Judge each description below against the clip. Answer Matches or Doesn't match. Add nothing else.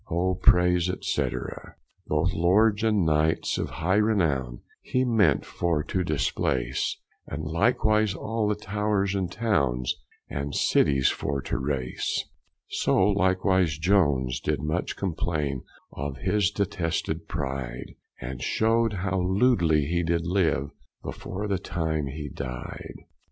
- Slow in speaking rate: Matches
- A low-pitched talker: Matches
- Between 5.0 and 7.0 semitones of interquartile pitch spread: Matches